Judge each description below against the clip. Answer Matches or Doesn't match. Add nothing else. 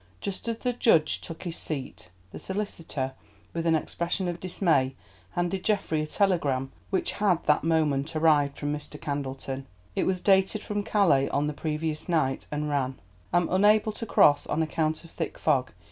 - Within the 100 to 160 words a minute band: Doesn't match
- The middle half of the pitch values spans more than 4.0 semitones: Matches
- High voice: Doesn't match